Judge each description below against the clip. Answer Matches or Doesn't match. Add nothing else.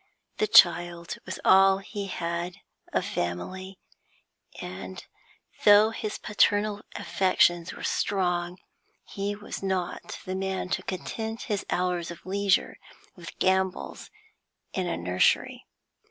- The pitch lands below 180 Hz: Doesn't match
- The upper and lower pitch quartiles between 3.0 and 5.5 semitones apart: Doesn't match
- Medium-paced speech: Doesn't match